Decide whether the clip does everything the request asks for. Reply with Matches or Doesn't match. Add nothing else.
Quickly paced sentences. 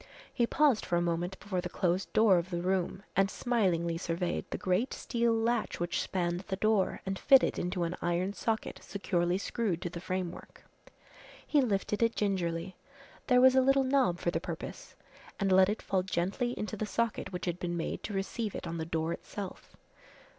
Doesn't match